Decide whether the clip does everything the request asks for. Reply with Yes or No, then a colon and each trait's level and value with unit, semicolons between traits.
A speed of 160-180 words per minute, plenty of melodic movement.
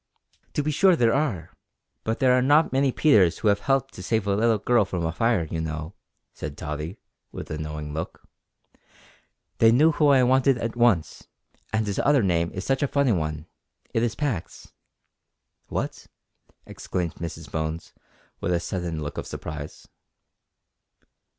Yes: average, 170 wpm; wide, 8.0 semitones